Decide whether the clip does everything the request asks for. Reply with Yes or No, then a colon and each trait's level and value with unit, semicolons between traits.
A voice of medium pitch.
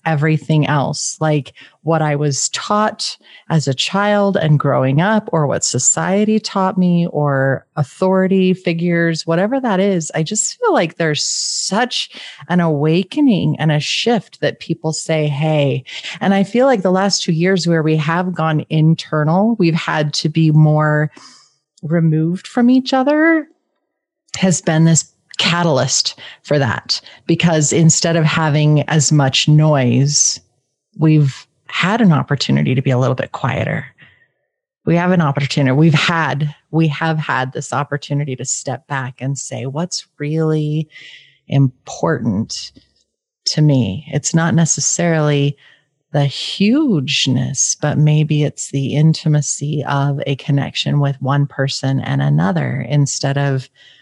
Yes: medium, 155 Hz